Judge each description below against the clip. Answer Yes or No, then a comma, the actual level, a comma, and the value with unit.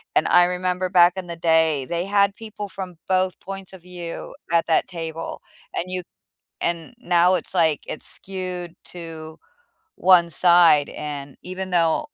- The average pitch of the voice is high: No, medium, 175 Hz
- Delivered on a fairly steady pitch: Yes, narrow, 2.0 semitones